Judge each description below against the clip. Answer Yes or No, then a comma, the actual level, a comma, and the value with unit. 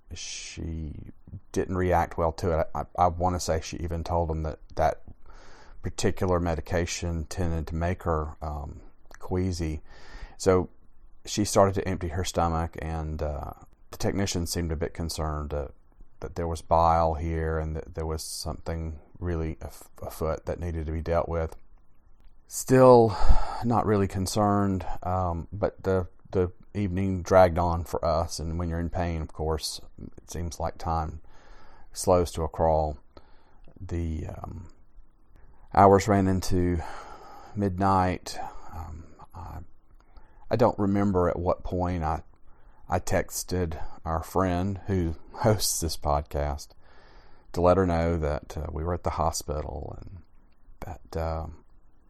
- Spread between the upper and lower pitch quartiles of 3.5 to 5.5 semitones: No, narrow, 2.6 semitones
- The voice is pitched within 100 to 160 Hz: No, very low, 85 Hz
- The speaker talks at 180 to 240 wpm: No, average, 145 wpm